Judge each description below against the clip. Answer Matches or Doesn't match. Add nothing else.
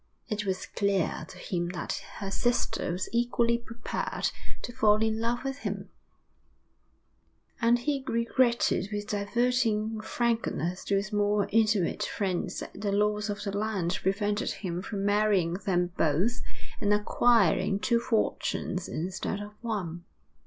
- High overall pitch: Matches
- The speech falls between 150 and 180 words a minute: Doesn't match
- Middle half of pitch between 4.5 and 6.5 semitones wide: Doesn't match